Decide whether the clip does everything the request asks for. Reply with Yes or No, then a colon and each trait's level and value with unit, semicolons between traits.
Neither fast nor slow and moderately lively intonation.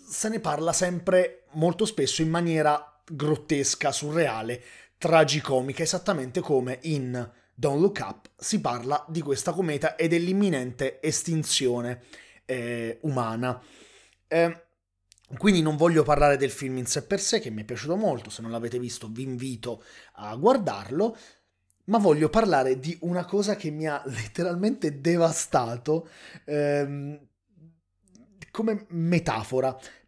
Yes: average, 130 wpm; average, 4.9 semitones